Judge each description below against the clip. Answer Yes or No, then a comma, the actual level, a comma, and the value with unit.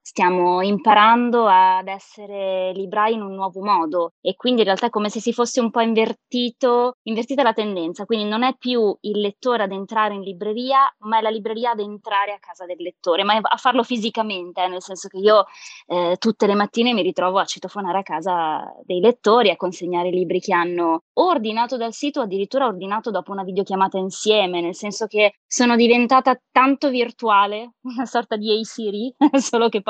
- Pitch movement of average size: Yes, average, 3.7 semitones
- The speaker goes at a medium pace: No, fast, 195 wpm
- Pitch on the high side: Yes, high, 215 Hz